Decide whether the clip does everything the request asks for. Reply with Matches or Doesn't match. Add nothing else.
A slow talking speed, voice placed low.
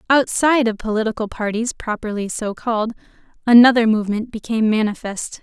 Doesn't match